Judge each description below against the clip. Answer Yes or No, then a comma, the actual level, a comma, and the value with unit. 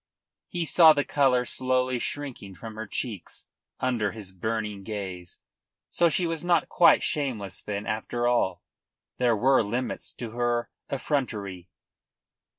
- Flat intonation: No, average, 4.6 semitones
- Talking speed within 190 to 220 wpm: No, slow, 135 wpm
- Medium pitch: No, low, 120 Hz